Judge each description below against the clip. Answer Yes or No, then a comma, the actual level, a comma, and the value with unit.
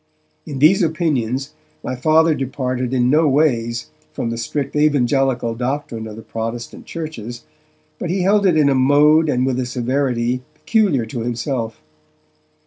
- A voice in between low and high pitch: No, low, 130 Hz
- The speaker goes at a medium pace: Yes, average, 150 wpm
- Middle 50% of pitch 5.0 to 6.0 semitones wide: No, average, 4.2 semitones